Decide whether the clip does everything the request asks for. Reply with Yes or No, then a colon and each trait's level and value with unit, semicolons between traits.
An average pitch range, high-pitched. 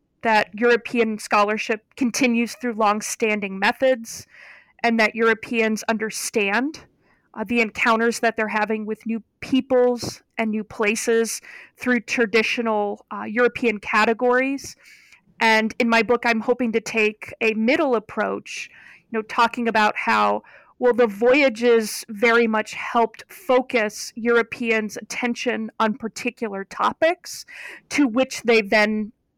No: narrow, 1.9 semitones; high, 230 Hz